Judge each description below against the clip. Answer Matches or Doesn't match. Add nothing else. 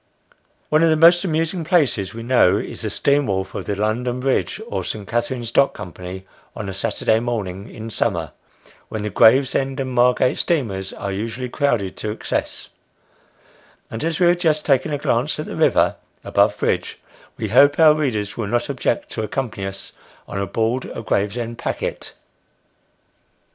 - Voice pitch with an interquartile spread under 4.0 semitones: Doesn't match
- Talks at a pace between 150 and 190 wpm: Matches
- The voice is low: Matches